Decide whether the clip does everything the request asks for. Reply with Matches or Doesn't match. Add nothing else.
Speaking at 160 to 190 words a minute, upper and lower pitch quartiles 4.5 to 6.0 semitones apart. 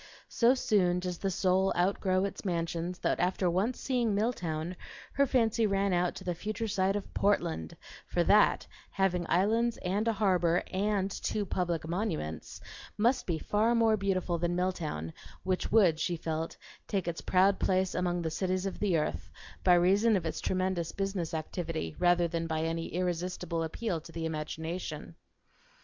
Doesn't match